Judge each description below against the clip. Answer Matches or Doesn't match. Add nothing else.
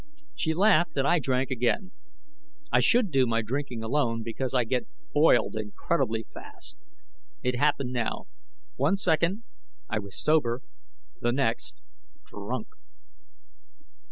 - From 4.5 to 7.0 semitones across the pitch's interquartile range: Matches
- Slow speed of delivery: Matches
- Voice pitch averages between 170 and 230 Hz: Doesn't match